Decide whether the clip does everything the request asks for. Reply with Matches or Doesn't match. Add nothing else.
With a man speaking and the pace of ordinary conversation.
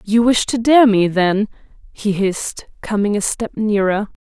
Doesn't match